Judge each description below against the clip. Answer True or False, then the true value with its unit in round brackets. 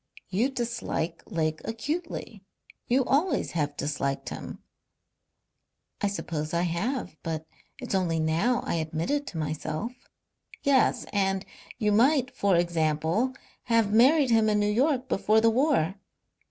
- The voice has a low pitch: False (210 Hz)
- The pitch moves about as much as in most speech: False (7.4 semitones)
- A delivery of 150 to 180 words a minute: False (135 wpm)